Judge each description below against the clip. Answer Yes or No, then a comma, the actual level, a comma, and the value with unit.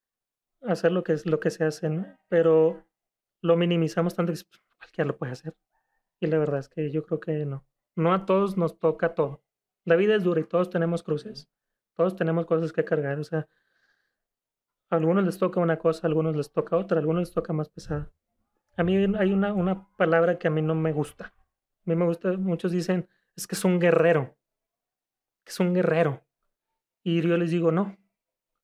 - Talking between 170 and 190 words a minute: No, fast, 205 wpm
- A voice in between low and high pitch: Yes, medium, 170 Hz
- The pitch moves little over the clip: Yes, narrow, 2.2 semitones